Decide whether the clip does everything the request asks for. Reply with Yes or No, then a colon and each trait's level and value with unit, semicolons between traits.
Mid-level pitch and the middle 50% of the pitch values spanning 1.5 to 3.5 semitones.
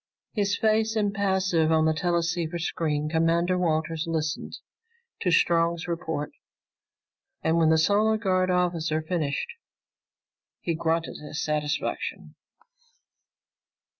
Yes: medium, 170 Hz; narrow, 2.6 semitones